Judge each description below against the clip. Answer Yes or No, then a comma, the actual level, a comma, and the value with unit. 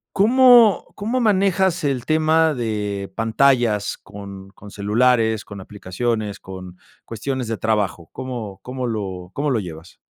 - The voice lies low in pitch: Yes, low, 115 Hz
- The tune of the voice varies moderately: No, wide, 6.1 semitones